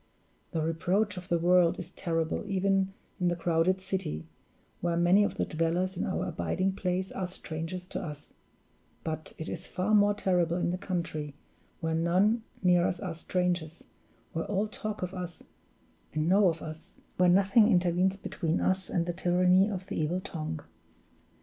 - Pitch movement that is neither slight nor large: No, narrow, 2.3 semitones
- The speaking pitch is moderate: Yes, medium, 180 Hz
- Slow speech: No, average, 170 wpm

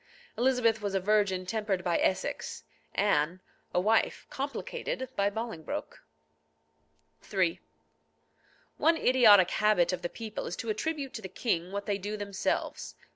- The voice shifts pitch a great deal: No, average, 3.4 semitones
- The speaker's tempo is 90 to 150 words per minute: Yes, slow, 135 wpm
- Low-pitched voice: No, high, 205 Hz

